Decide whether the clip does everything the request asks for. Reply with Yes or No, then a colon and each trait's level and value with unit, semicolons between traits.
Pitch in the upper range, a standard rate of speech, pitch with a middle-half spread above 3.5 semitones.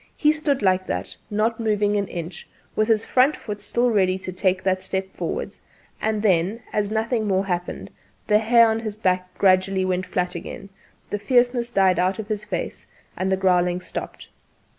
No: high, 200 Hz; average, 185 wpm; average, 2.9 semitones